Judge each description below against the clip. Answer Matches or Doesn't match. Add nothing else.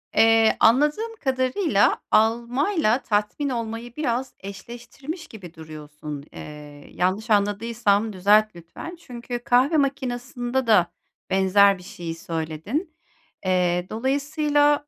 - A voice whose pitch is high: Matches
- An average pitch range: Doesn't match